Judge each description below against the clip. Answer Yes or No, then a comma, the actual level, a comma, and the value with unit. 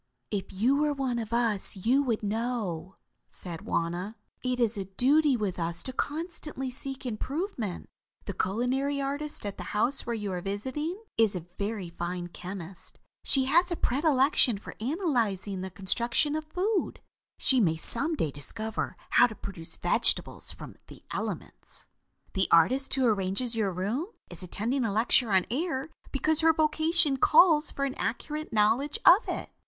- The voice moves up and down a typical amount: No, wide, 6.4 semitones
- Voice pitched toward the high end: Yes, high, 240 Hz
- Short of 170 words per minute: Yes, average, 160 wpm